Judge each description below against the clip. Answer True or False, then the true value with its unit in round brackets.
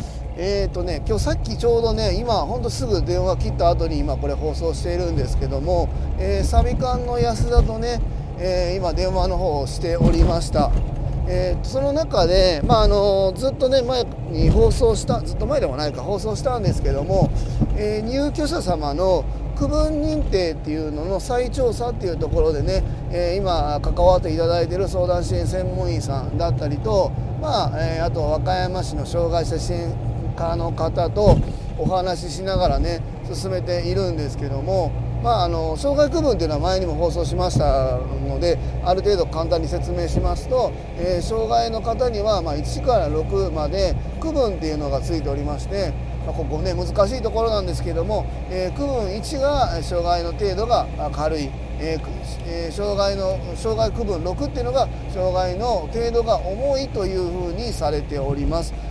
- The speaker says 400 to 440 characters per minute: False (340 characters per minute)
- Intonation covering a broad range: True (8.1 semitones)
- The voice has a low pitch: False (170 Hz)